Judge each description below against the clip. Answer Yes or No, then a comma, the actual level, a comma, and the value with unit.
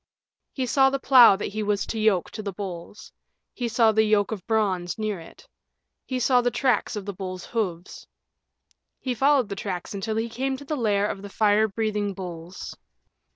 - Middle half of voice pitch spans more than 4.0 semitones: No, average, 3.4 semitones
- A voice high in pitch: Yes, high, 215 Hz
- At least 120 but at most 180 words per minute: No, average, 195 wpm